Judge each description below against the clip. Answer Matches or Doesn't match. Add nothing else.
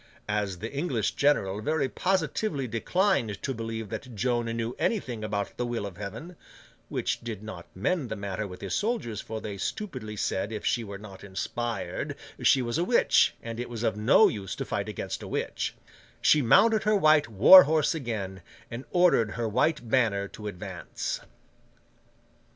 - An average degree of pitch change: Doesn't match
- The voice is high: Doesn't match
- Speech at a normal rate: Matches